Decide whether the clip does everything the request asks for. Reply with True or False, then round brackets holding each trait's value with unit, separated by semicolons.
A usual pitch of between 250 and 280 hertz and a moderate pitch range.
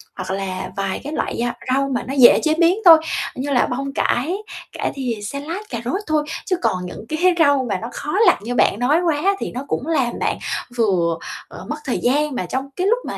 True (270 Hz; 4.6 semitones)